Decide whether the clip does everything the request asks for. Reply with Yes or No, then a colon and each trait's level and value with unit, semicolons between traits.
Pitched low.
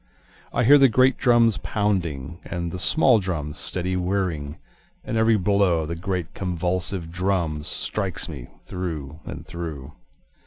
Yes: very low, 90 Hz